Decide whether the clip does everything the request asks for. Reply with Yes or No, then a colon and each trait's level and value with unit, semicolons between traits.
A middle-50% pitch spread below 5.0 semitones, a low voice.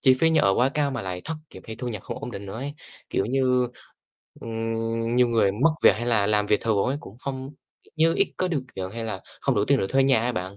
Yes: average, 4.2 semitones; low, 115 Hz